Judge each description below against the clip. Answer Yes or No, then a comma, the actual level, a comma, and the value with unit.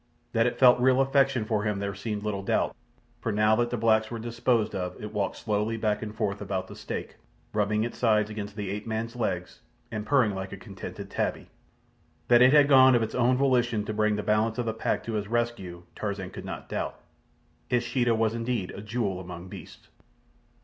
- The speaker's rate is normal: No, fast, 210 wpm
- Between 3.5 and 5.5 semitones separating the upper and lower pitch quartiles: No, narrow, 2.5 semitones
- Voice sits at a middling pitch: No, low, 110 Hz